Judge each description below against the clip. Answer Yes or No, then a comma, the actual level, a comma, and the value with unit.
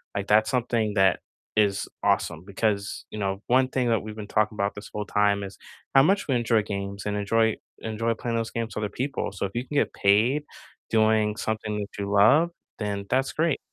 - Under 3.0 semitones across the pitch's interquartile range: Yes, narrow, 2.4 semitones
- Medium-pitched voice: No, low, 110 Hz